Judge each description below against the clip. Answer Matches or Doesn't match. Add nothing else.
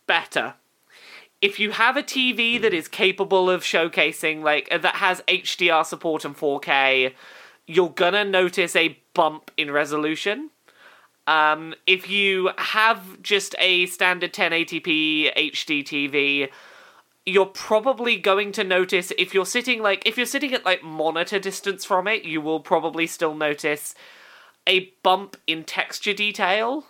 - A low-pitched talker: Doesn't match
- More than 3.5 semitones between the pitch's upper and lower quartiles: Matches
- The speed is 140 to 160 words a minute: Matches